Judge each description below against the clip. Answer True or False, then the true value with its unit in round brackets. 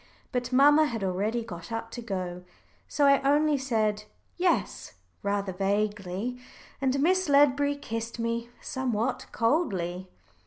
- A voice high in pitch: True (230 Hz)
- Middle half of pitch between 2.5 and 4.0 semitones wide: False (5.4 semitones)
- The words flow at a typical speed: False (125 wpm)